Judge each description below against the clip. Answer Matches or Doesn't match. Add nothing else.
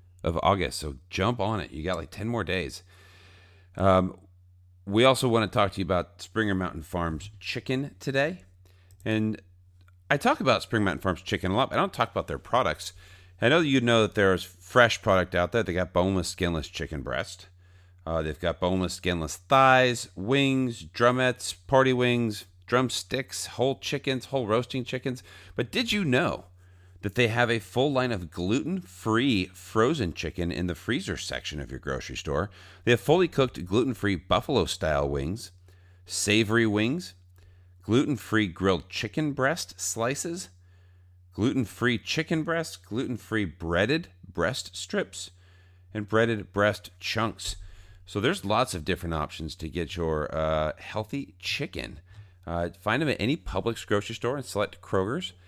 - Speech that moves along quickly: Doesn't match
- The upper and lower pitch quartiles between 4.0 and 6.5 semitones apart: Matches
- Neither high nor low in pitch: Doesn't match